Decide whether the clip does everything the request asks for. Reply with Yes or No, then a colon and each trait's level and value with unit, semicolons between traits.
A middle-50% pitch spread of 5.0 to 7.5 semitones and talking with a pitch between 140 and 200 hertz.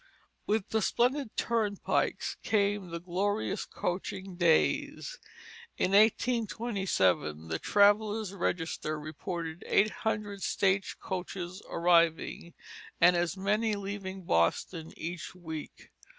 No: average, 3.5 semitones; high, 190 Hz